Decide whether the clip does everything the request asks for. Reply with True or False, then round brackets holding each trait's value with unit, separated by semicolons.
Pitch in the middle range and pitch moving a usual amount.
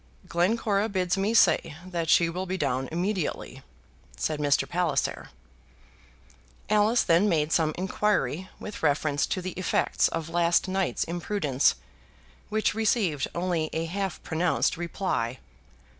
True (175 Hz; 3.5 semitones)